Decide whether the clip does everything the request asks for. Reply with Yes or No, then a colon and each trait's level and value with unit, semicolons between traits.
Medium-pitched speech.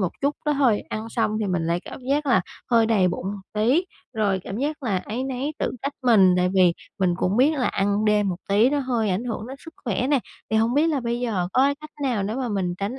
No: high, 225 Hz